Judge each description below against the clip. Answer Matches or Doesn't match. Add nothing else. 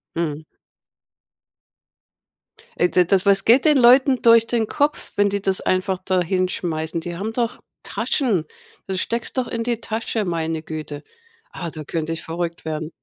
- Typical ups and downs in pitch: Doesn't match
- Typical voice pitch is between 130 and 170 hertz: Doesn't match